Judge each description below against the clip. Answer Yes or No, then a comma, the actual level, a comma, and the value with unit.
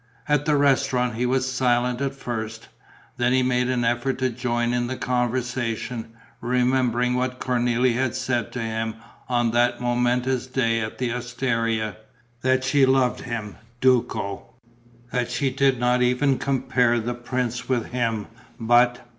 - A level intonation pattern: Yes, narrow, 1.3 semitones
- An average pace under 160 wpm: Yes, average, 150 wpm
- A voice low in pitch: Yes, low, 125 Hz